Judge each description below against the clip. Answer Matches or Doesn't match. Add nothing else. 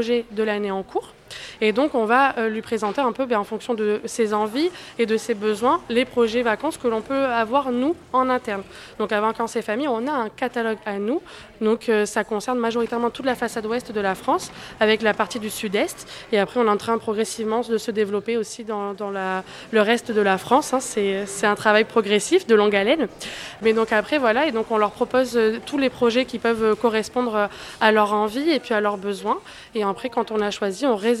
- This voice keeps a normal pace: Doesn't match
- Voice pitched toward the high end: Matches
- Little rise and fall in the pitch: Matches